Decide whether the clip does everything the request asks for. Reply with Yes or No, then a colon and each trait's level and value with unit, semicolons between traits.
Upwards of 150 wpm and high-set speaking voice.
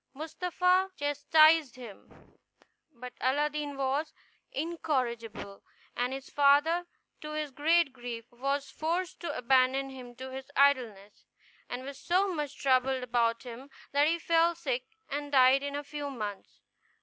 No: slow, 135 wpm; very high, 275 Hz